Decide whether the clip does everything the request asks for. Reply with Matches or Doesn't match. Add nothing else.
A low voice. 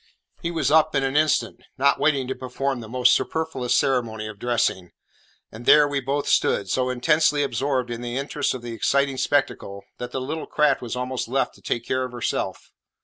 Matches